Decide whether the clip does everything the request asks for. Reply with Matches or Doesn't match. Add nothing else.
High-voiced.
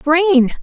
Matches